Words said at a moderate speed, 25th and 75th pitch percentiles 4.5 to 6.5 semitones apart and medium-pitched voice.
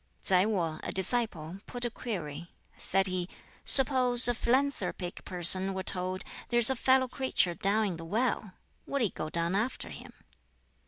No: average, 160 wpm; average, 5.2 semitones; high, 195 Hz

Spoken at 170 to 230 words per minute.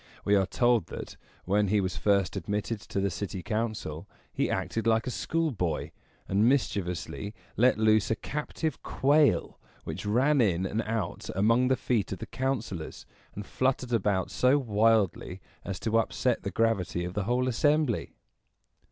No: average, 160 wpm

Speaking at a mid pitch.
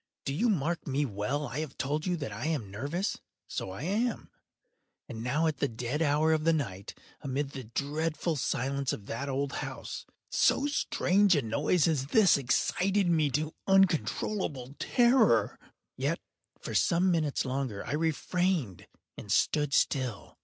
Yes: medium, 150 Hz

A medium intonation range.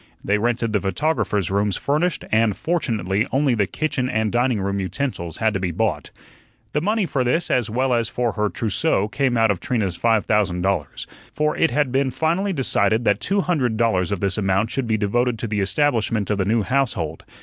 Yes: average, 4.8 semitones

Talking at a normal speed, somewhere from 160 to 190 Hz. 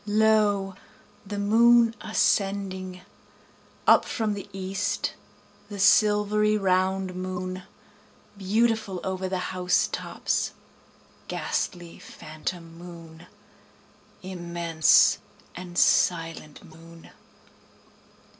No: slow, 80 wpm; medium, 185 Hz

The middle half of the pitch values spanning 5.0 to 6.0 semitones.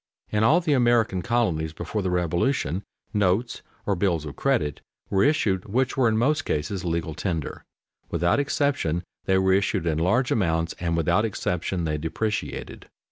Yes: wide, 5.6 semitones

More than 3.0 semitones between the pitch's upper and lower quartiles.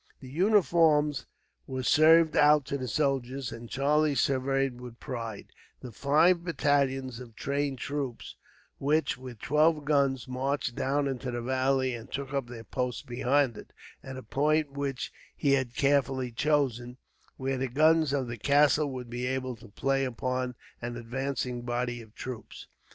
No: narrow, 2.5 semitones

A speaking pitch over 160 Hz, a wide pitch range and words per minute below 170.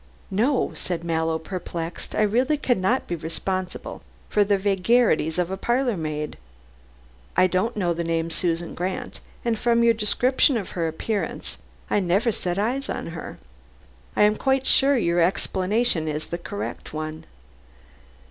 Yes: high, 190 Hz; wide, 5.7 semitones; average, 150 wpm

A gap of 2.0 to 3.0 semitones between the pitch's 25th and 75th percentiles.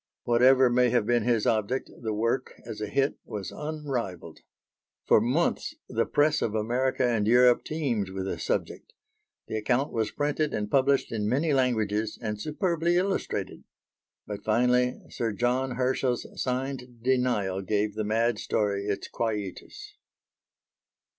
No: average, 3.7 semitones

